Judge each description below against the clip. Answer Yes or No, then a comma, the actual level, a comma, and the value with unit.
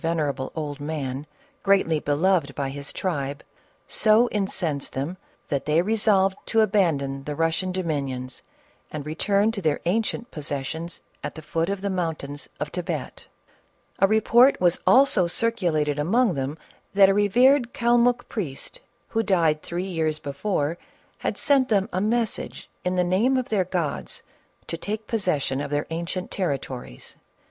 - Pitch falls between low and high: Yes, medium, 175 Hz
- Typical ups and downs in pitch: No, wide, 5.9 semitones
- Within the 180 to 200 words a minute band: No, average, 155 wpm